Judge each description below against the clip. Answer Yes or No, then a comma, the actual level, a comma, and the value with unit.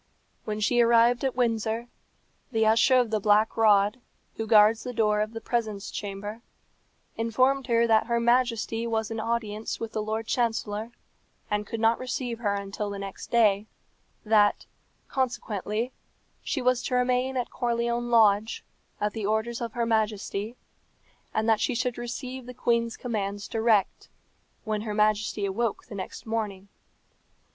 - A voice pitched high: Yes, high, 225 Hz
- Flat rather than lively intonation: Yes, narrow, 2.0 semitones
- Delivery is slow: No, average, 155 wpm